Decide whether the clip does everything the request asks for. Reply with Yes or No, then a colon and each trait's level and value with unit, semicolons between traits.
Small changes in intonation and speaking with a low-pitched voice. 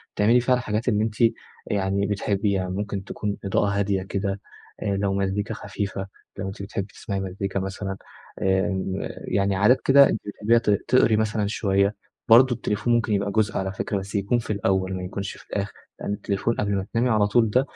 Yes: narrow, 1.9 semitones; low, 100 Hz